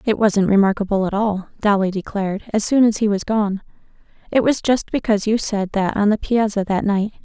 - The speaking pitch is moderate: No, high, 205 Hz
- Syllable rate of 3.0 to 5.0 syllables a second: No, 5.5 syllables/s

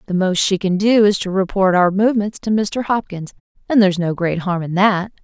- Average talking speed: No, fast, 230 wpm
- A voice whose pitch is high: Yes, high, 195 Hz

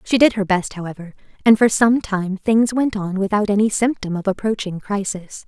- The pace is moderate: Yes, average, 195 wpm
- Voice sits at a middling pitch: No, high, 205 Hz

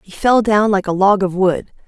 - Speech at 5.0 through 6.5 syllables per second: No, 4.8 syllables/s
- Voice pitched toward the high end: Yes, high, 200 Hz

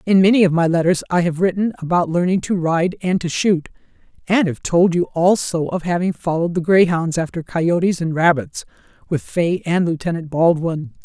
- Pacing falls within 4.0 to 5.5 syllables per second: Yes, 5.2 syllables/s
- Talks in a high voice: No, medium, 170 Hz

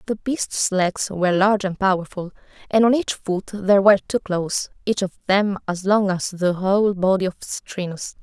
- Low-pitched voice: No, high, 195 Hz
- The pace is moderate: Yes, average, 190 wpm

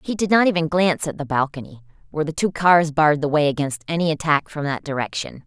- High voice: No, medium, 155 Hz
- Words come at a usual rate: No, fast, 230 wpm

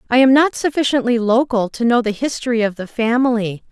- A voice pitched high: Yes, high, 240 Hz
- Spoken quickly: No, average, 195 wpm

